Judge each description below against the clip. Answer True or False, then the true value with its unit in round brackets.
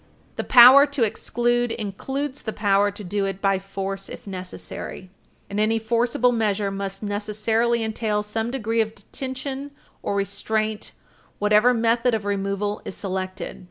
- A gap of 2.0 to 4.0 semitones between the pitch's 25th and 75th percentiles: True (3.0 semitones)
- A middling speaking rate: True (145 wpm)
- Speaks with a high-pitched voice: True (215 Hz)